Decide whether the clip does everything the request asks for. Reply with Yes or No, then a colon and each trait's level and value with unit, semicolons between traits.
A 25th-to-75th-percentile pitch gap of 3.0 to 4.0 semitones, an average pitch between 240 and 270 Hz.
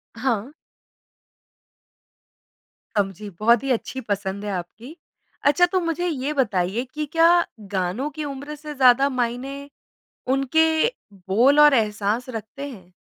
No: wide, 5.5 semitones; very high, 255 Hz